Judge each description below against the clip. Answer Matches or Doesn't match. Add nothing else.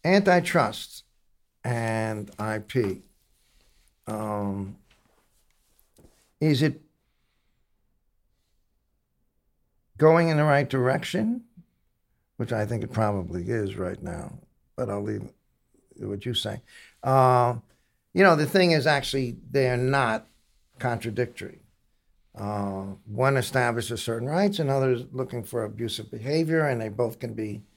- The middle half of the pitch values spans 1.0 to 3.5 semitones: Doesn't match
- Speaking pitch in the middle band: Doesn't match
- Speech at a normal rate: Doesn't match